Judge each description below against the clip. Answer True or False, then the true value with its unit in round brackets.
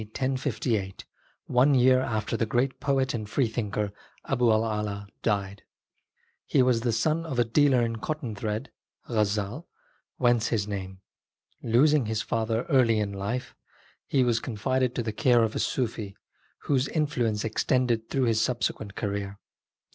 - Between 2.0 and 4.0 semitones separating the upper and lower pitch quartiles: True (3.3 semitones)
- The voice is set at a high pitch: False (115 Hz)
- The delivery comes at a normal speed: True (155 wpm)